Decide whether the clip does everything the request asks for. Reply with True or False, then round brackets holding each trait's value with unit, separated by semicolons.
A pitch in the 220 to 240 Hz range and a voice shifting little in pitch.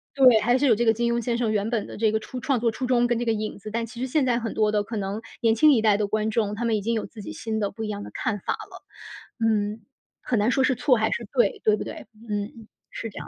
True (225 Hz; 2.0 semitones)